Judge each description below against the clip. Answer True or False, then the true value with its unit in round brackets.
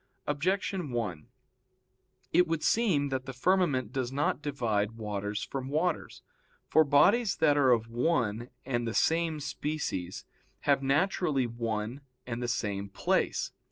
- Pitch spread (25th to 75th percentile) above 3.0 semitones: True (5.1 semitones)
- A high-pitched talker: False (135 Hz)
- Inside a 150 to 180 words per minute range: False (135 wpm)